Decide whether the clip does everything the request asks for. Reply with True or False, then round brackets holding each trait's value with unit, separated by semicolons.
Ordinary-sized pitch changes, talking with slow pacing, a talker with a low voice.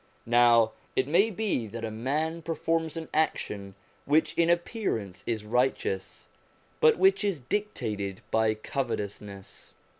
False (7.3 semitones; 125 wpm; 125 Hz)